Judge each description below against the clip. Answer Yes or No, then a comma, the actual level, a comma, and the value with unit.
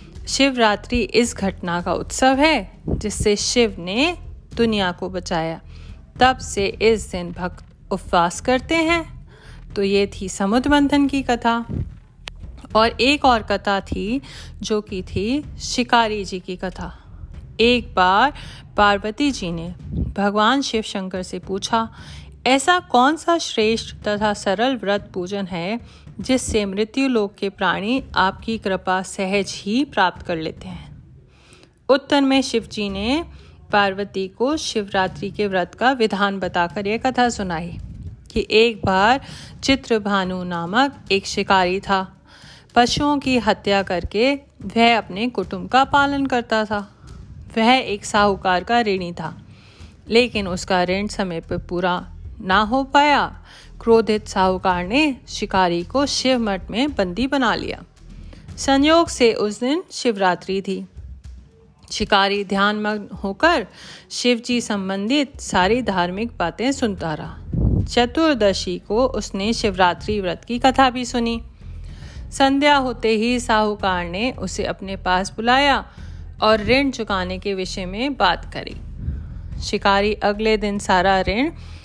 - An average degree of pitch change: Yes, average, 4.6 semitones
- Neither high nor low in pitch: No, high, 210 Hz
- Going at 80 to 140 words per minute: Yes, average, 130 wpm